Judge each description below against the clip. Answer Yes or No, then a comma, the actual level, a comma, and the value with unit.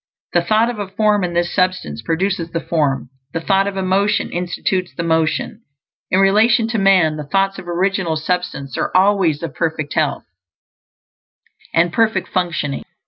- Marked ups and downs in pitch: No, average, 3.1 semitones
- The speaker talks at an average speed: Yes, average, 170 wpm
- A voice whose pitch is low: No, medium, 180 Hz